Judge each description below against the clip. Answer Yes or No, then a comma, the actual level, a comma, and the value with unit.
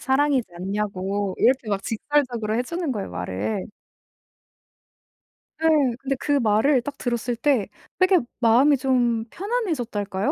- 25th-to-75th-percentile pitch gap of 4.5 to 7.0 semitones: Yes, average, 5.2 semitones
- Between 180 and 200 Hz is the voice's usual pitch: No, high, 240 Hz